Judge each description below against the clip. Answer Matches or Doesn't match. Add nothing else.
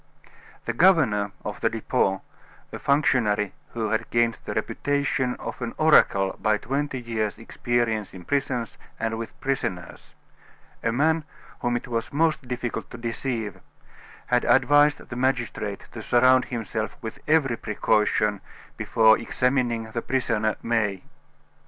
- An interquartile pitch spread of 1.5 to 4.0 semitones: Matches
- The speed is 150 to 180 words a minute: Doesn't match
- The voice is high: Doesn't match